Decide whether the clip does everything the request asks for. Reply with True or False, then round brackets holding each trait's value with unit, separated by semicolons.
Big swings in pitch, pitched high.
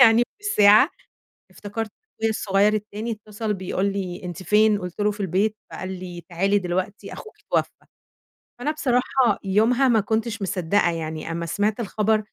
False (2.9 semitones; 205 Hz)